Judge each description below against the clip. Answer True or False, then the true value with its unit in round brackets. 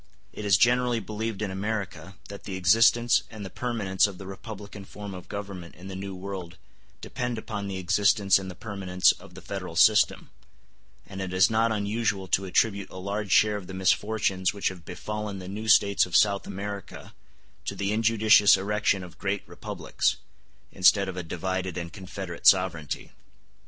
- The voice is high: False (100 Hz)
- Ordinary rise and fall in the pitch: False (2.2 semitones)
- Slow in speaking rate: False (175 wpm)